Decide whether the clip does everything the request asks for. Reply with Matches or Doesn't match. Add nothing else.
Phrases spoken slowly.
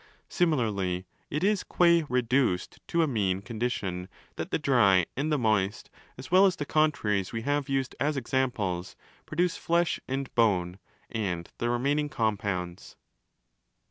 Doesn't match